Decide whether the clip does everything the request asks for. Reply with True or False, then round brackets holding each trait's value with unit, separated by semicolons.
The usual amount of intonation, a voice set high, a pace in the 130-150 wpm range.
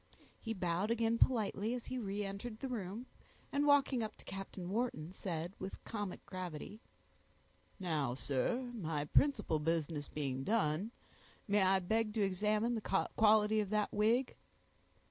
True (4.3 semitones; 205 Hz; 145 wpm)